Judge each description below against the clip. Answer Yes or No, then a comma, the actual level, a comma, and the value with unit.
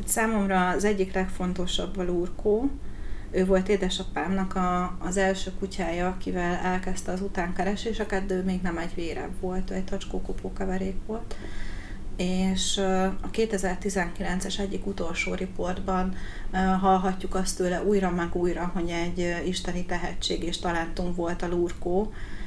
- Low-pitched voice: No, medium, 185 Hz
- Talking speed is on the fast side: No, average, 130 wpm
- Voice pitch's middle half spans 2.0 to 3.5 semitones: No, narrow, 1.4 semitones